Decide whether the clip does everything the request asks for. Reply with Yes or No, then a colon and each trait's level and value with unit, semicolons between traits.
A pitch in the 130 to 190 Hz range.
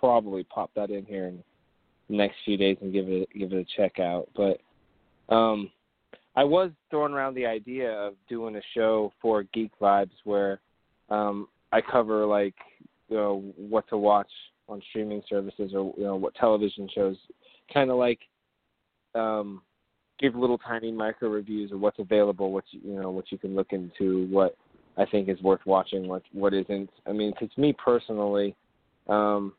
No: low, 105 Hz